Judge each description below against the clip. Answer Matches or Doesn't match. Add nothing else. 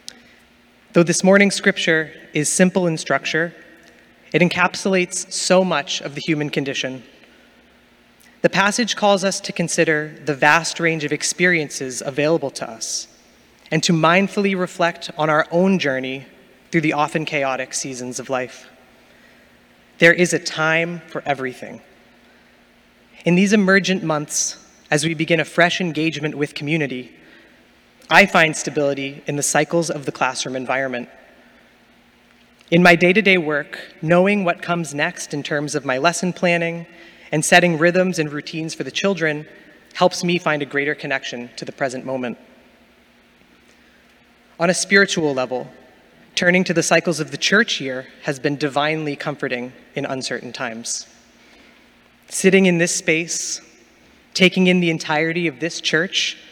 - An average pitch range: Matches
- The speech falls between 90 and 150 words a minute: Matches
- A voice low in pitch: Doesn't match